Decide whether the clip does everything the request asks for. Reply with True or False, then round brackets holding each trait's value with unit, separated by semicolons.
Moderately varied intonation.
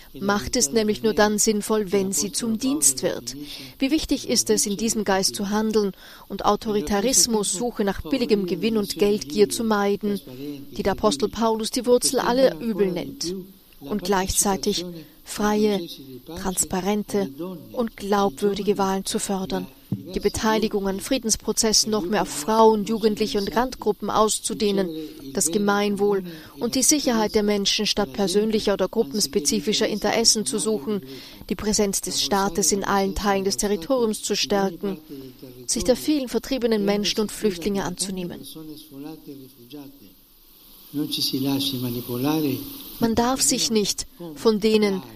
True (3.0 semitones)